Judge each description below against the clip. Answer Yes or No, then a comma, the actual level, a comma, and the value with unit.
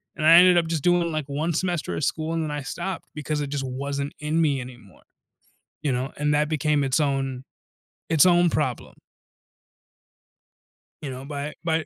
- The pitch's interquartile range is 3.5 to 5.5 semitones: No, average, 2.8 semitones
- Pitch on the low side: No, medium, 150 Hz